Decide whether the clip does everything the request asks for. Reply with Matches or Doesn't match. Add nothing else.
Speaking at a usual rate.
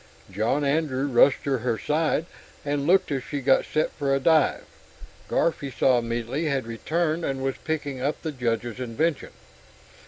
Matches